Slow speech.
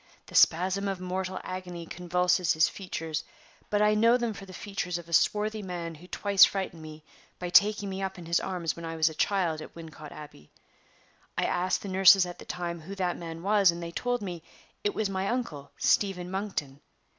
No: fast, 205 wpm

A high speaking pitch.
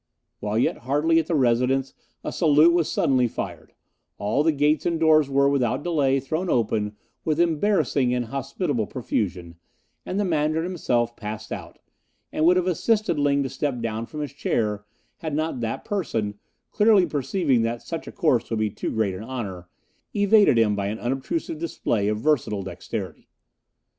No: low, 135 Hz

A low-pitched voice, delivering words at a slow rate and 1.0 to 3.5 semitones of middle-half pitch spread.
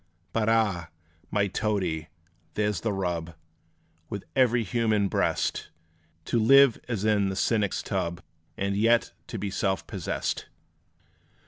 Yes: low, 105 Hz; slow, 125 wpm; average, 2.8 semitones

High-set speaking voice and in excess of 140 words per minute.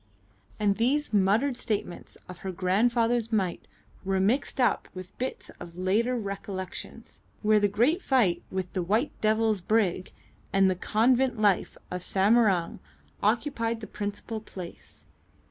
No: high, 210 Hz; slow, 135 wpm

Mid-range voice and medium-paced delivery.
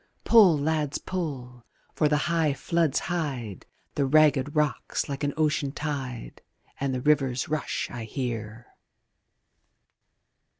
No: medium, 145 Hz; slow, 120 wpm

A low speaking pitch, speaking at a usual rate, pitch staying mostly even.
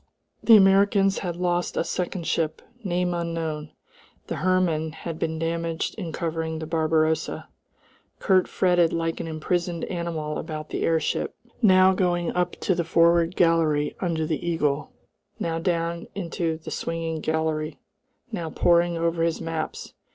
No: medium, 165 Hz; average, 145 wpm; narrow, 1.6 semitones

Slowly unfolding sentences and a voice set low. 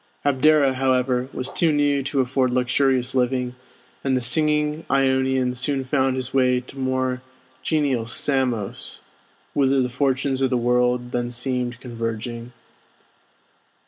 Yes: slow, 130 wpm; low, 130 Hz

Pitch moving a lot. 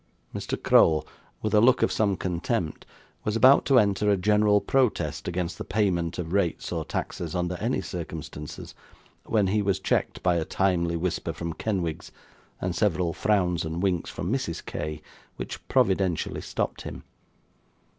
No: average, 3.6 semitones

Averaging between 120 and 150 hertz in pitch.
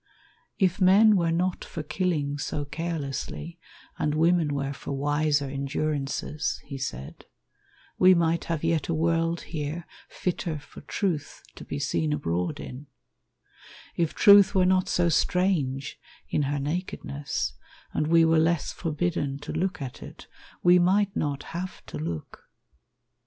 No: medium, 160 Hz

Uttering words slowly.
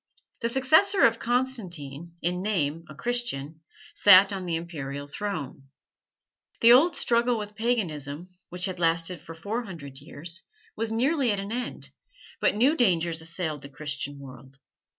No: average, 150 wpm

